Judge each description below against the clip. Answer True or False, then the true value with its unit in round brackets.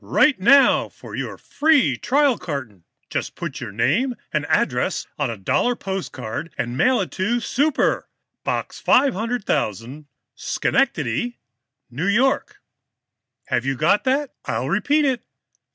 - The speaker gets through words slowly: True (130 wpm)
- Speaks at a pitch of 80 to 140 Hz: False (195 Hz)